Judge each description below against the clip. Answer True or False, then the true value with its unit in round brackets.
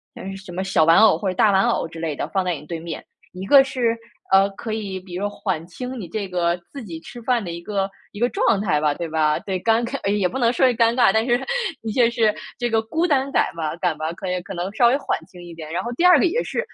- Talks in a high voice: True (195 Hz)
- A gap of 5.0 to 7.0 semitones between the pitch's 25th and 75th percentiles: True (5.3 semitones)